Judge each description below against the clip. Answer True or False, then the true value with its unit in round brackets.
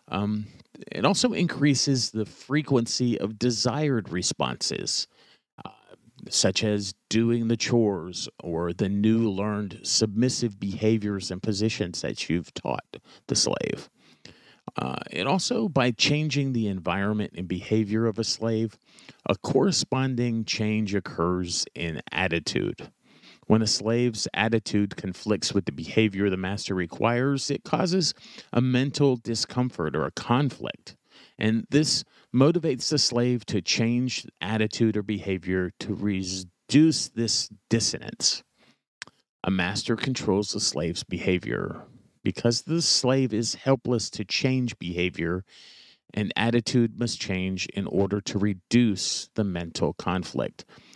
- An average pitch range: True (4.2 semitones)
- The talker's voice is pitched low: True (110 Hz)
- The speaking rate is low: True (120 wpm)